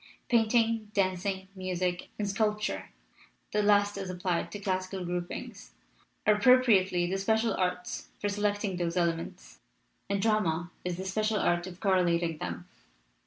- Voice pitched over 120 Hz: Yes, high, 190 Hz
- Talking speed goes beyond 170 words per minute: No, slow, 135 wpm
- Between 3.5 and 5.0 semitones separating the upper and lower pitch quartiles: No, average, 2.8 semitones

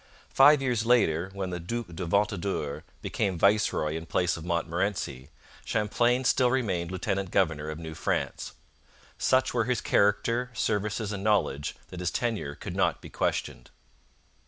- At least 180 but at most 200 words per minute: No, average, 150 wpm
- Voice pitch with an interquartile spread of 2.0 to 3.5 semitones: No, wide, 5.4 semitones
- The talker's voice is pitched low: Yes, low, 100 Hz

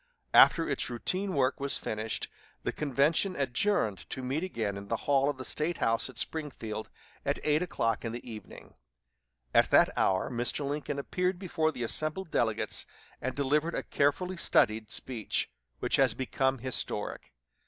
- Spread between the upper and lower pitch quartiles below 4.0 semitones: No, average, 5.0 semitones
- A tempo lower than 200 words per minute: Yes, average, 160 wpm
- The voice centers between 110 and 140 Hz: Yes, low, 135 Hz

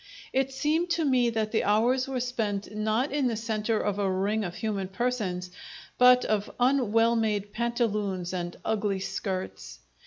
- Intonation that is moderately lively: Yes, average, 3.6 semitones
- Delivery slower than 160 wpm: No, average, 165 wpm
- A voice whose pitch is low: No, high, 220 Hz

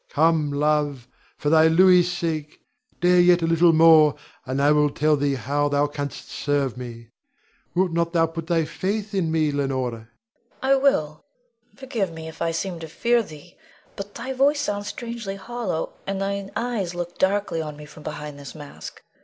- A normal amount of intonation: Yes, average, 4.7 semitones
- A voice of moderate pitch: Yes, medium, 165 Hz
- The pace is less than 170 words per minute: No, average, 180 wpm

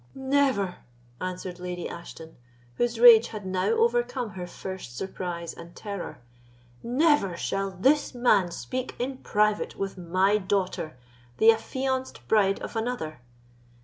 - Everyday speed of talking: No, slow, 120 wpm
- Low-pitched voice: No, high, 195 Hz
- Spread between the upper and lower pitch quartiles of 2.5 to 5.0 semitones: No, wide, 5.4 semitones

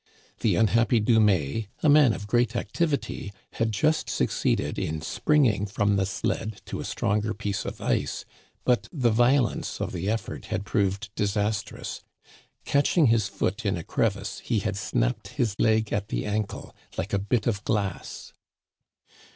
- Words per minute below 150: No, average, 155 wpm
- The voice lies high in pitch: No, low, 110 Hz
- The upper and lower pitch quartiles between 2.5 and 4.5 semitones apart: Yes, average, 2.8 semitones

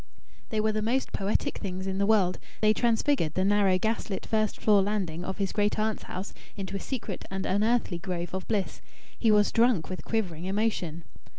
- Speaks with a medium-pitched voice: No, high, 200 Hz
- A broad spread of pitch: No, narrow, 2.6 semitones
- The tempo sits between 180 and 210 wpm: Yes, average, 190 wpm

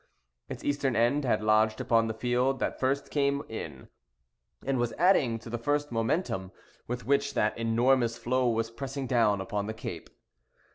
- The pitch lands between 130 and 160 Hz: No, low, 120 Hz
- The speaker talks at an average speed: Yes, average, 170 wpm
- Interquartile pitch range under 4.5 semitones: Yes, average, 3.4 semitones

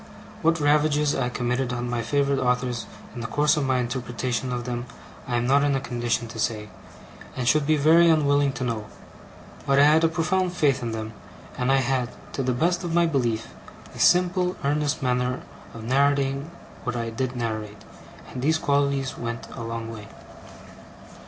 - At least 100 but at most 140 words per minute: No, average, 185 wpm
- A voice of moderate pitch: No, low, 130 Hz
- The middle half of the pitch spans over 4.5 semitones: No, average, 3.3 semitones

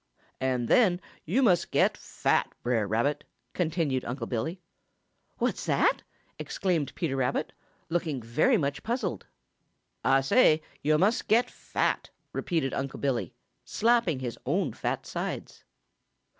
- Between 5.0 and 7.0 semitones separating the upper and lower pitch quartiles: Yes, wide, 5.6 semitones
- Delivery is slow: Yes, slow, 125 wpm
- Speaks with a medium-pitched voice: Yes, medium, 145 Hz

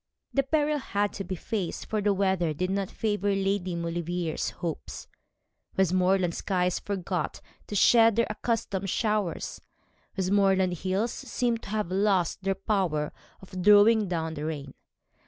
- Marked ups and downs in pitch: No, average, 2.7 semitones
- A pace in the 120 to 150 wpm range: Yes, average, 140 wpm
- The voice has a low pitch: No, high, 195 Hz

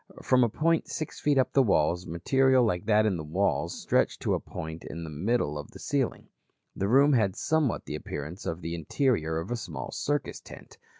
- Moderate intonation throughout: No, wide, 8.2 semitones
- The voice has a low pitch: Yes, low, 100 Hz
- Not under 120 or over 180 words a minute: No, fast, 205 wpm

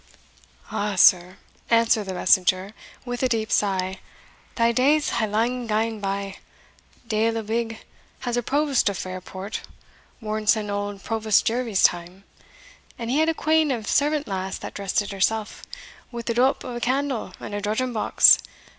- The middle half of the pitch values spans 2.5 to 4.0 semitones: Yes, average, 3.4 semitones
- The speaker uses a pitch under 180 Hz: No, high, 220 Hz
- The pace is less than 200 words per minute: Yes, average, 165 wpm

